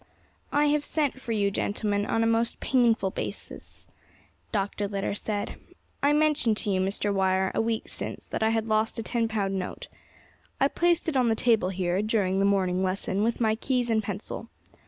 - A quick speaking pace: No, average, 190 wpm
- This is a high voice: Yes, high, 220 Hz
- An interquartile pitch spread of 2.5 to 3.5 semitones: Yes, average, 3.0 semitones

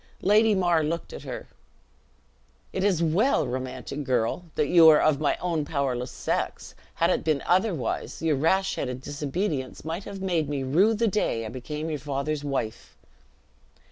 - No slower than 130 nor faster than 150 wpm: No, average, 165 wpm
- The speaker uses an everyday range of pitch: Yes, average, 4.8 semitones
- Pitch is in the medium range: Yes, medium, 155 Hz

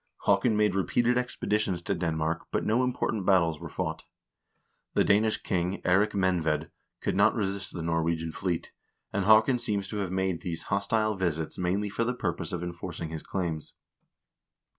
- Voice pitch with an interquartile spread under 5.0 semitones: Yes, average, 3.7 semitones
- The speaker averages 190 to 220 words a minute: No, average, 165 wpm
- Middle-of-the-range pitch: No, very low, 95 Hz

